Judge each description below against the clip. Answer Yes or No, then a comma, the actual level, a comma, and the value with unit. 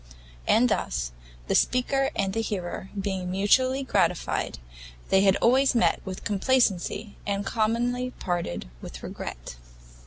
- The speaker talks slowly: Yes, slow, 125 wpm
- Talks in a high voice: Yes, high, 205 Hz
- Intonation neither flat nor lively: Yes, average, 4.7 semitones